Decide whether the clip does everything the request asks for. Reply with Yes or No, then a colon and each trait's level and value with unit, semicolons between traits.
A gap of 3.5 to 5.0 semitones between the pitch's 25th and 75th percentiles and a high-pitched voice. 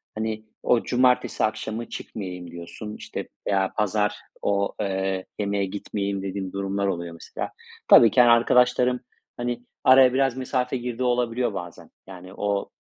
No: average, 4.1 semitones; low, 105 Hz